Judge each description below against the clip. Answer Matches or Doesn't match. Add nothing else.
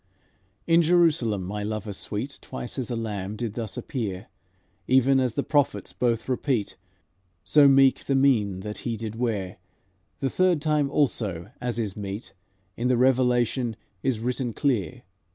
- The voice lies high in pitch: Doesn't match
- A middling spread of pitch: Matches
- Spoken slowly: Doesn't match